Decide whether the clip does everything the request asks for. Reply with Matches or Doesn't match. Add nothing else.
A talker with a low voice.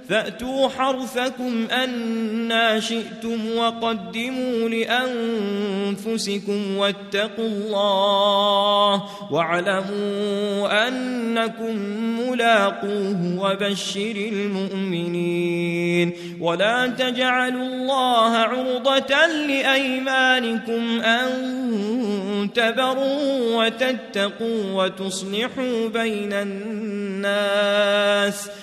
Doesn't match